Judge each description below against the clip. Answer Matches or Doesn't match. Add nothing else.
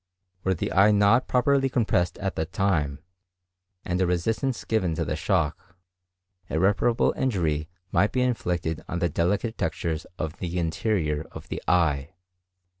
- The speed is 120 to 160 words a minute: Matches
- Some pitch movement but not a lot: Matches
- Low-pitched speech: Matches